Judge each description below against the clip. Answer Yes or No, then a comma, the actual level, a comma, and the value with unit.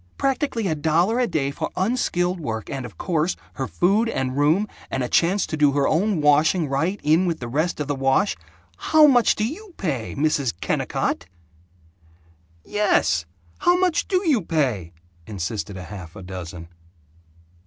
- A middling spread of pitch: No, wide, 7.9 semitones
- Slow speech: No, average, 165 wpm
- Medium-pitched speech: Yes, medium, 155 Hz